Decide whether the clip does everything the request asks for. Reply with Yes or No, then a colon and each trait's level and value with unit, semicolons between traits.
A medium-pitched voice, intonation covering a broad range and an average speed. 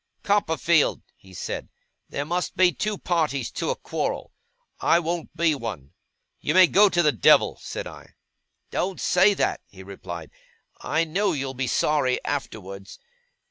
Yes: medium, 155 Hz; wide, 7.4 semitones; average, 150 wpm